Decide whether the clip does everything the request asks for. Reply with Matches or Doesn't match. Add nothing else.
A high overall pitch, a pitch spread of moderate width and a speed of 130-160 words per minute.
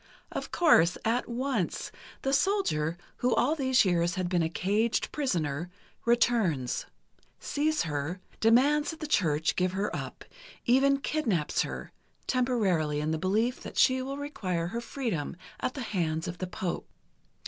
Doesn't match